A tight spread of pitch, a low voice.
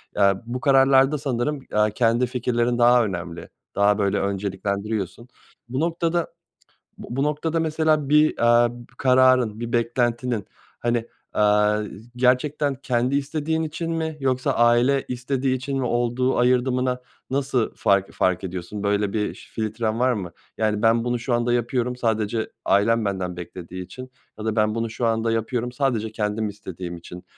No: average, 3.6 semitones; low, 120 Hz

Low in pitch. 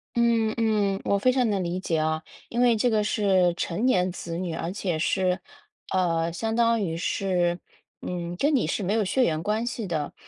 No: high, 190 Hz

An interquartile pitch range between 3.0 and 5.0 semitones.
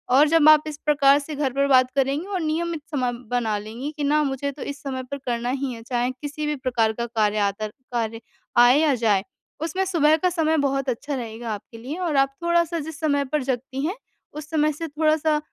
Yes: average, 3.8 semitones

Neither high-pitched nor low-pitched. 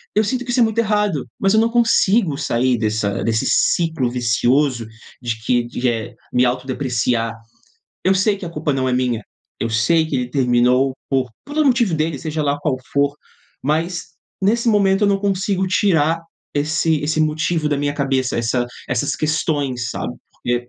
Yes: medium, 145 Hz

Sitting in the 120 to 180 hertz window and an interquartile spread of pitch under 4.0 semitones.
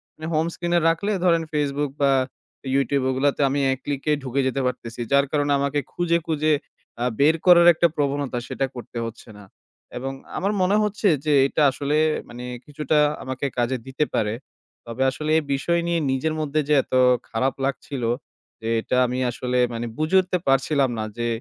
Yes: medium, 140 Hz; average, 3.2 semitones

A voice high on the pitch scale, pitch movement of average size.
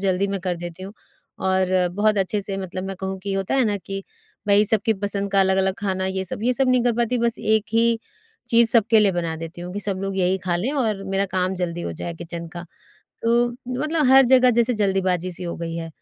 Yes: high, 195 Hz; average, 3.3 semitones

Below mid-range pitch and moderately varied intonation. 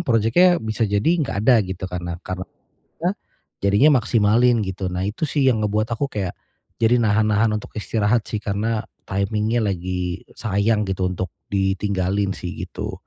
Yes: low, 105 Hz; average, 3.0 semitones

